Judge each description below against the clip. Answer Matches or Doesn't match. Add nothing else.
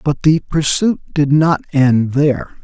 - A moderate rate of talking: Matches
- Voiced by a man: Matches